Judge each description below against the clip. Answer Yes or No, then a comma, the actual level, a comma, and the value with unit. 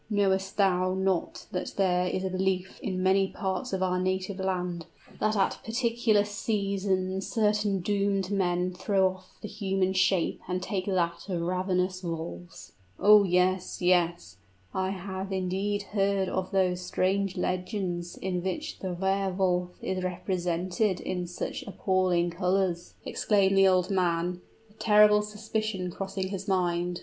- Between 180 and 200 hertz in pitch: Yes, high, 190 Hz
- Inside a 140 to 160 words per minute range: Yes, average, 145 wpm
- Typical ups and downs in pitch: No, narrow, 1.5 semitones